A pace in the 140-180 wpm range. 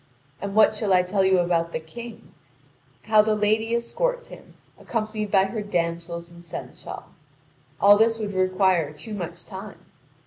Yes: average, 160 wpm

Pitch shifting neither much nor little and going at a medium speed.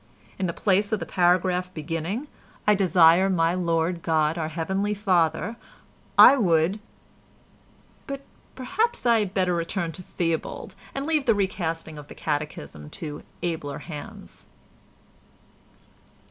No: average, 3.8 semitones; slow, 125 wpm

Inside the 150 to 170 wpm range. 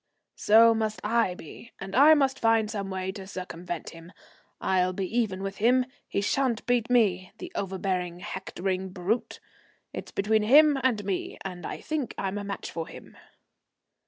Yes: average, 165 wpm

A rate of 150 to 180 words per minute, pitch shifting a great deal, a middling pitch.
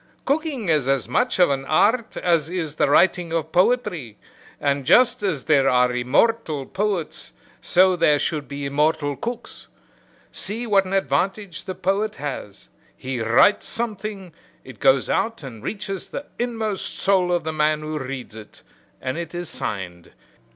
Yes: average, 160 wpm; wide, 6.4 semitones; medium, 165 Hz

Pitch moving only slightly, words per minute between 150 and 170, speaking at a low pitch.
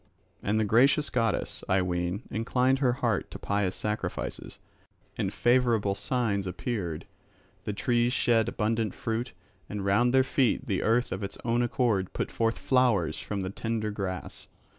No: average, 3.7 semitones; average, 155 wpm; low, 110 Hz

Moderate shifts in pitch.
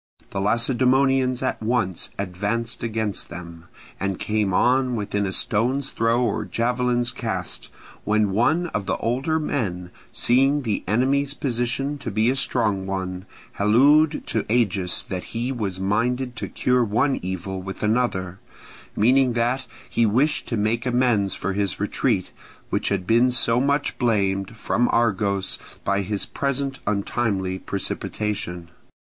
Yes: average, 4.3 semitones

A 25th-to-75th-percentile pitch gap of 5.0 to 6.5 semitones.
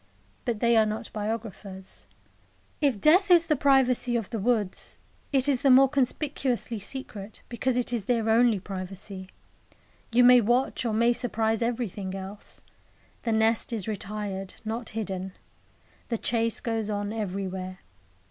No: average, 3.3 semitones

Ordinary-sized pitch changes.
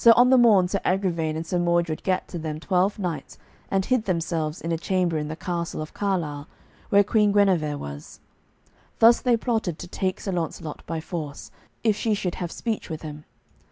Yes: average, 4.1 semitones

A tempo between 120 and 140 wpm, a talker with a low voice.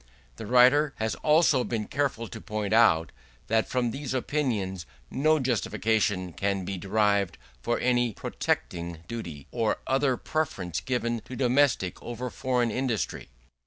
Yes: slow, 135 wpm; low, 115 Hz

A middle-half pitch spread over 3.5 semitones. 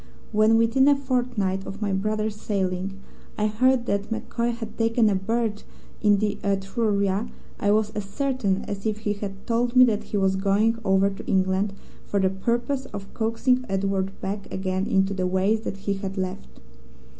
No: average, 2.7 semitones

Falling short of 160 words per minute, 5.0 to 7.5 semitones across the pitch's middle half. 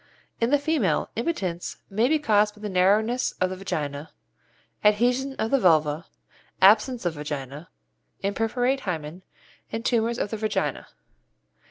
Yes: average, 140 wpm; wide, 5.4 semitones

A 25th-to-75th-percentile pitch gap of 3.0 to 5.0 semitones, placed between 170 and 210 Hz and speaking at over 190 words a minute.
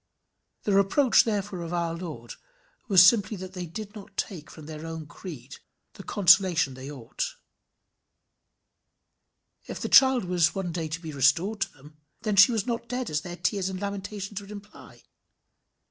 No: average, 4.1 semitones; medium, 185 Hz; average, 165 wpm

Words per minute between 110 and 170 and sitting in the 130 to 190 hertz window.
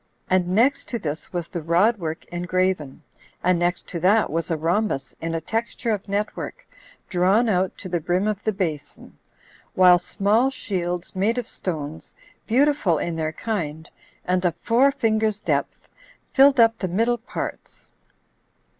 Yes: average, 160 wpm; medium, 185 Hz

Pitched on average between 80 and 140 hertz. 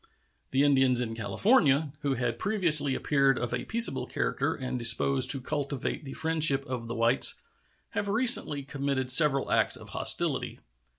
Yes: low, 135 Hz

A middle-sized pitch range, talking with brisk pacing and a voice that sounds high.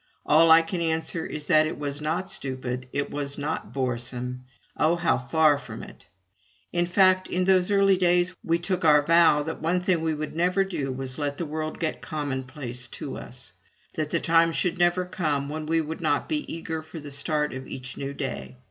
No: average, 3.4 semitones; fast, 210 wpm; medium, 155 Hz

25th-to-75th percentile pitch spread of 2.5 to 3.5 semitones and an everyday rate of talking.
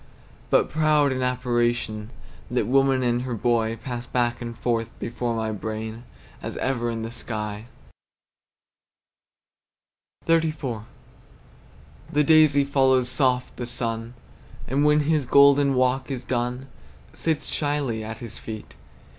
No: average, 3.1 semitones; slow, 125 wpm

